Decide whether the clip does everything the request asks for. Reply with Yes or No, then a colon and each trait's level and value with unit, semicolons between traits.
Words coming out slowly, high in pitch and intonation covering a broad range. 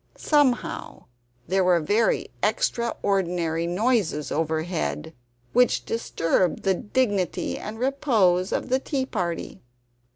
Yes: slow, 105 wpm; high, 195 Hz; wide, 6.1 semitones